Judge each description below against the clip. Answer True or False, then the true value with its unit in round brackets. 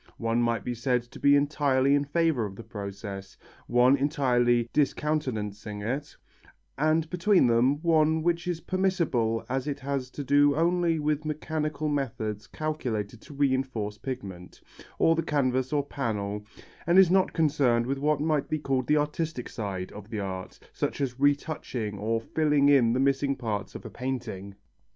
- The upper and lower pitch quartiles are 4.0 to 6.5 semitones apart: True (4.8 semitones)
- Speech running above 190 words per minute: False (165 wpm)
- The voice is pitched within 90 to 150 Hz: True (135 Hz)